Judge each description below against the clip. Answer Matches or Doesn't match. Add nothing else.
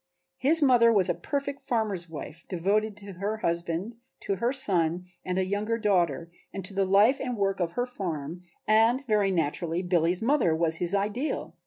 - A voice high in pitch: Matches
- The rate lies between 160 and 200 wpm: Matches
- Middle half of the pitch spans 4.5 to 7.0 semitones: Matches